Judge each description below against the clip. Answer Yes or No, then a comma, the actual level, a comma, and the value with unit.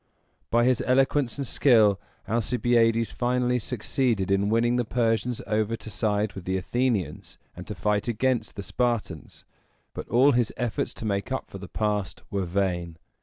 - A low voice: Yes, low, 115 Hz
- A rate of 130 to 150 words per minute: No, average, 165 wpm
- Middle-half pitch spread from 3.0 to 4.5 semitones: Yes, average, 3.6 semitones